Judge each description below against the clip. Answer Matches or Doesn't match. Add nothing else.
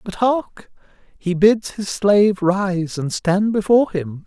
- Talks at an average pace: Matches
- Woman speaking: Doesn't match